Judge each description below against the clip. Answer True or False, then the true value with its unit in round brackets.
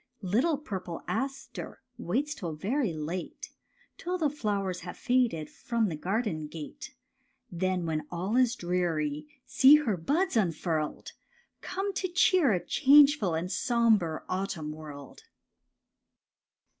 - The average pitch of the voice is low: False (190 Hz)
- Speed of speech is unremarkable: False (125 wpm)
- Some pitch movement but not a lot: False (8.1 semitones)